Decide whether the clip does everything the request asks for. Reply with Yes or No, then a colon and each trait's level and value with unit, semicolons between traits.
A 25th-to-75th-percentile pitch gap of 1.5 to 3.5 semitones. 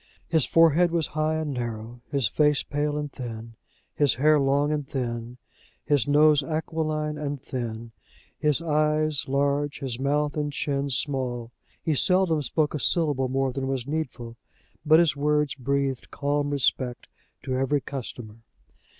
Yes: average, 2.8 semitones